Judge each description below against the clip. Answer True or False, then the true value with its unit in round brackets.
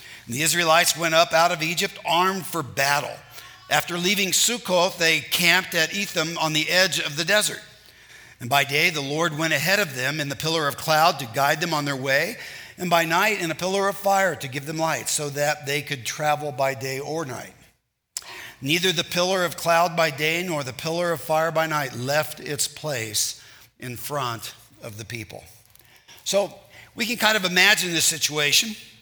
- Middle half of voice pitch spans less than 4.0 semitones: True (3.6 semitones)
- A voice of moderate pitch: True (160 Hz)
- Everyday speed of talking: True (195 wpm)